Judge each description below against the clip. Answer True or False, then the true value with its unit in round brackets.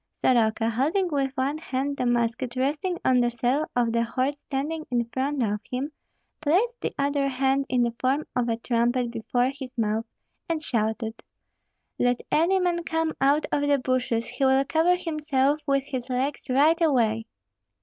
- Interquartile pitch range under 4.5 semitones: True (3.4 semitones)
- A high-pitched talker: True (265 Hz)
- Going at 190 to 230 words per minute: False (170 wpm)